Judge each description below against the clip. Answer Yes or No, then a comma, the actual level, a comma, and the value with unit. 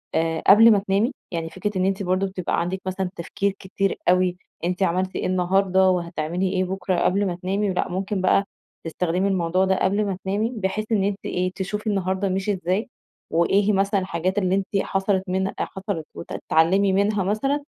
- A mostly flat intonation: Yes, narrow, 1.5 semitones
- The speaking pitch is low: No, high, 190 Hz